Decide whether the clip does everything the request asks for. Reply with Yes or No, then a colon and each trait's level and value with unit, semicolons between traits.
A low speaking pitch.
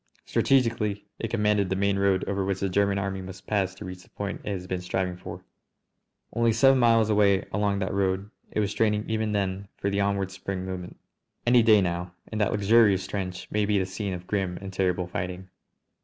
Yes: low, 100 Hz